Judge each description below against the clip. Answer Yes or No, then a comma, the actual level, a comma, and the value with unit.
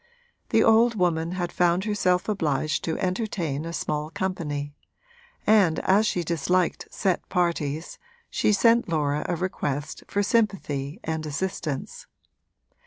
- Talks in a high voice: No, medium, 175 Hz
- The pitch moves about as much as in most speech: Yes, average, 3.9 semitones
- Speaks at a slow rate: Yes, slow, 125 wpm